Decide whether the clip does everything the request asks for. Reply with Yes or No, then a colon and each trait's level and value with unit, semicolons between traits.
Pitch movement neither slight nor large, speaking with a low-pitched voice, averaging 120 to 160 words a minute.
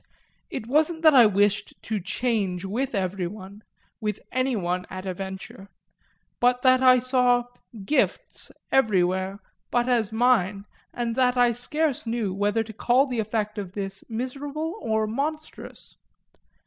No: average, 4.4 semitones; high, 225 Hz; slow, 135 wpm